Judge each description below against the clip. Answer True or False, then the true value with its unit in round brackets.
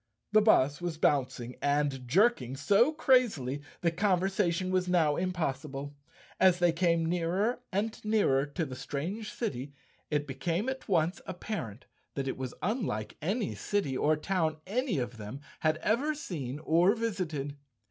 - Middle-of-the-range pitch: True (170 Hz)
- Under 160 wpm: True (145 wpm)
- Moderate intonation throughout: False (6.3 semitones)